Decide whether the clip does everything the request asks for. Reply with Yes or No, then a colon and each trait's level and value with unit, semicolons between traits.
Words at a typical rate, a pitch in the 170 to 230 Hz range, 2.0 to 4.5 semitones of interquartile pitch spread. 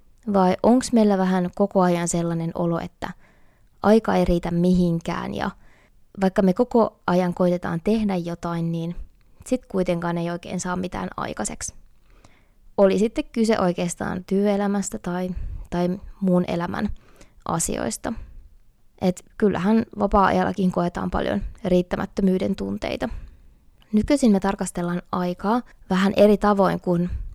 Yes: average, 120 wpm; medium, 185 Hz; narrow, 2.6 semitones